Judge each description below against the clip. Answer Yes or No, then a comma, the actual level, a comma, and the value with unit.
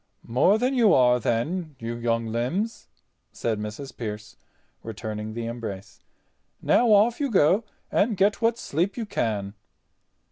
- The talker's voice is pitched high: No, low, 125 Hz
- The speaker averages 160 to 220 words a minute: No, average, 140 wpm